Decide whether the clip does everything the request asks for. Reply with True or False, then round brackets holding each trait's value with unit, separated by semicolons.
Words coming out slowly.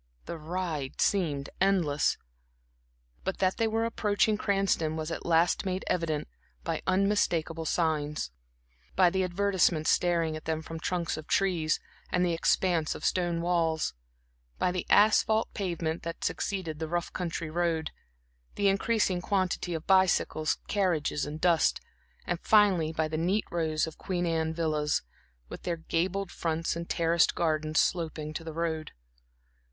False (145 wpm)